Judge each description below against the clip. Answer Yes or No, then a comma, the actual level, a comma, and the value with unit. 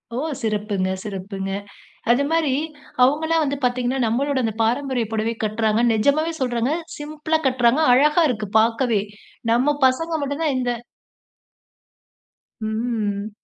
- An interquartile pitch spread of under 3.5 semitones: No, average, 4.6 semitones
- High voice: Yes, high, 245 Hz